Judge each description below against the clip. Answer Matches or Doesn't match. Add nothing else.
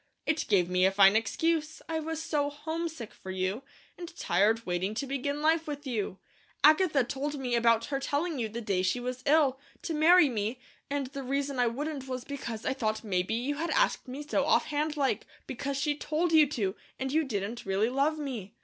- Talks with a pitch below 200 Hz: Doesn't match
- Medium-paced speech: Matches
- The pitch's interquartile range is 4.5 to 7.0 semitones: Matches